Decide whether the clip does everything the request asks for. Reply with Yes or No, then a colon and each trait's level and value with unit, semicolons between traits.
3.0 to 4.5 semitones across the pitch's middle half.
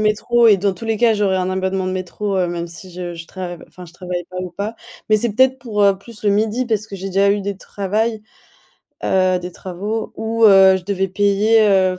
No: narrow, 2.6 semitones